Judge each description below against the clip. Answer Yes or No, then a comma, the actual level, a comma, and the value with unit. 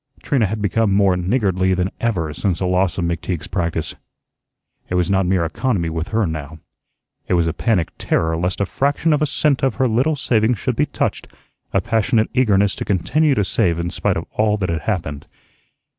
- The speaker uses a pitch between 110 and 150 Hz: No, very low, 95 Hz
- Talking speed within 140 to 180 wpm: No, average, 200 wpm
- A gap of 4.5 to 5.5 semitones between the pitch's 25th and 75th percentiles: Yes, average, 4.8 semitones